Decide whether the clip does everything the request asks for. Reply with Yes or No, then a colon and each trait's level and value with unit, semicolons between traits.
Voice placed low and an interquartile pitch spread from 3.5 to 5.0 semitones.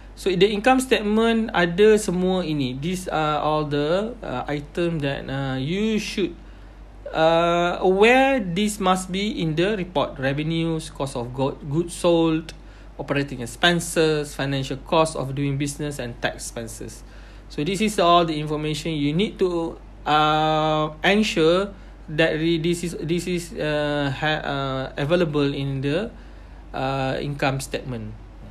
No: medium, 155 Hz; average, 4.2 semitones